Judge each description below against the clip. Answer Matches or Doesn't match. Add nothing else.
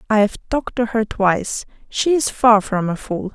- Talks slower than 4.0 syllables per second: Doesn't match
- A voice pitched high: Matches